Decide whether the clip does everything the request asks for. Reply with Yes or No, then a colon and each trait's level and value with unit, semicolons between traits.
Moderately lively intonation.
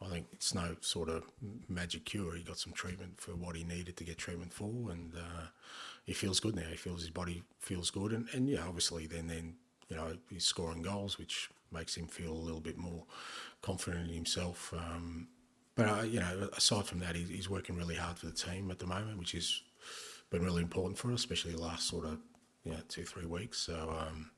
No: narrow, 2.3 semitones